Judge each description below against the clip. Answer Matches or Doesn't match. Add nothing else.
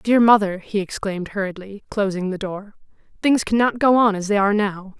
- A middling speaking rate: Matches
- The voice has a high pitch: Matches